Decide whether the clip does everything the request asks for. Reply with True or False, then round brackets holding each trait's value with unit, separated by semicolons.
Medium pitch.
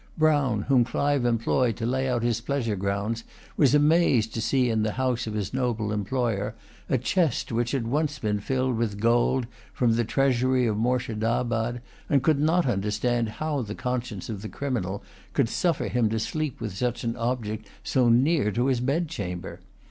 False (120 Hz)